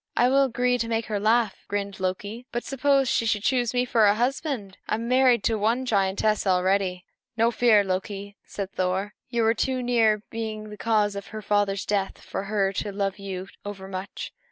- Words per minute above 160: Yes, fast, 205 wpm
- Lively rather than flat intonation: No, average, 3.2 semitones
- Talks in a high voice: Yes, high, 215 Hz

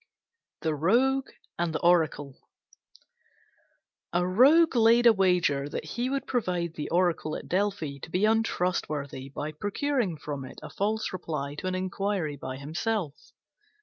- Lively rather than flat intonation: Yes, wide, 6.3 semitones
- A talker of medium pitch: Yes, medium, 180 Hz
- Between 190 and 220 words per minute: No, average, 145 wpm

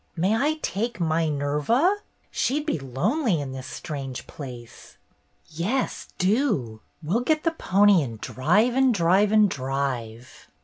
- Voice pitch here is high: No, medium, 175 Hz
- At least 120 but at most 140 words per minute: Yes, slow, 135 wpm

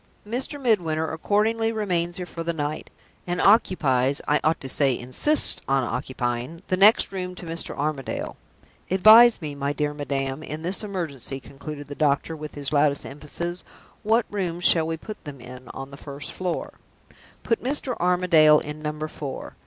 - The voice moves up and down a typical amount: Yes, average, 4.5 semitones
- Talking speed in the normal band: Yes, average, 170 wpm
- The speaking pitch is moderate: Yes, medium, 155 Hz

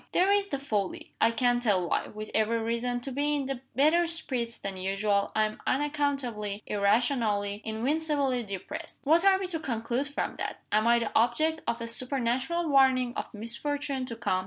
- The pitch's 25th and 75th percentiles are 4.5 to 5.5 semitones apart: Yes, average, 4.8 semitones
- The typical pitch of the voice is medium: No, high, 245 Hz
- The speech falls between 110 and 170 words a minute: No, average, 180 wpm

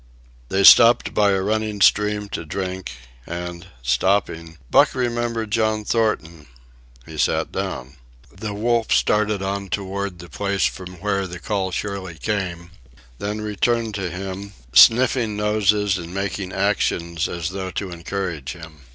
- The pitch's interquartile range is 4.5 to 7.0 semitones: No, average, 3.1 semitones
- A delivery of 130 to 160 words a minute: Yes, average, 140 wpm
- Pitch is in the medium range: No, low, 100 Hz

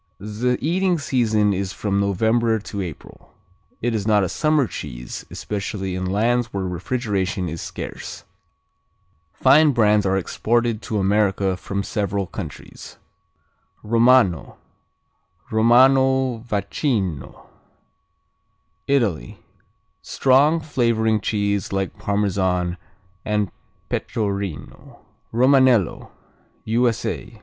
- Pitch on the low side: Yes, low, 105 Hz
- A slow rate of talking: Yes, slow, 95 wpm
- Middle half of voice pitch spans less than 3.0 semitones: No, average, 3.8 semitones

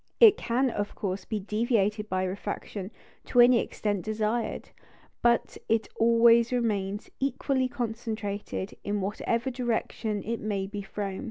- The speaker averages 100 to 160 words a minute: Yes, slow, 135 wpm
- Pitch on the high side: Yes, high, 220 Hz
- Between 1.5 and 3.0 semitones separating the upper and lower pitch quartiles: Yes, narrow, 2.6 semitones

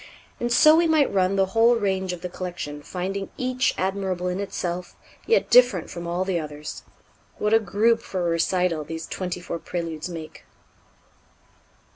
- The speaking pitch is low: No, medium, 185 Hz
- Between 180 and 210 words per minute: No, average, 165 wpm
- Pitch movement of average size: Yes, average, 3.4 semitones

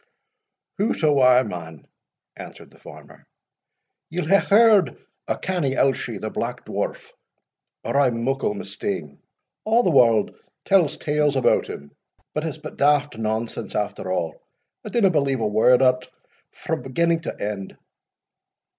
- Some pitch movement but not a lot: No, wide, 6.5 semitones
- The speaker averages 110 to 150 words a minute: Yes, average, 145 wpm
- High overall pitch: No, low, 135 Hz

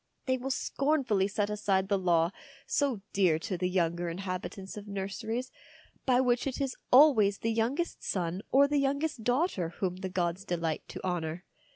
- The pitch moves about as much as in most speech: No, wide, 5.9 semitones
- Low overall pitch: No, high, 200 Hz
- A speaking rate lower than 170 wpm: No, average, 175 wpm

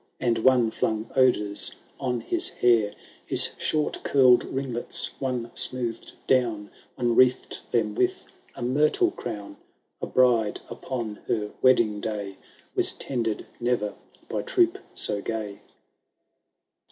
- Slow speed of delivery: Yes, slow, 120 wpm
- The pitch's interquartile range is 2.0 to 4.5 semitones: Yes, average, 3.1 semitones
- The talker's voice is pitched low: Yes, low, 120 Hz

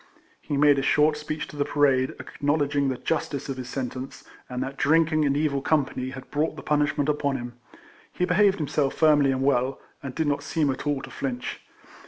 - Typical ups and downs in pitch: No, narrow, 2.1 semitones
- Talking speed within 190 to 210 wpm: Yes, fast, 205 wpm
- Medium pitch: Yes, medium, 145 Hz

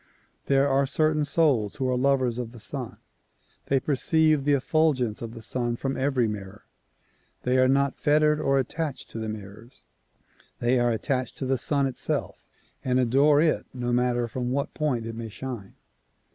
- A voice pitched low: Yes, low, 130 Hz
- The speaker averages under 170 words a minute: No, average, 175 wpm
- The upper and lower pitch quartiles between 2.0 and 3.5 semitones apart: Yes, average, 2.9 semitones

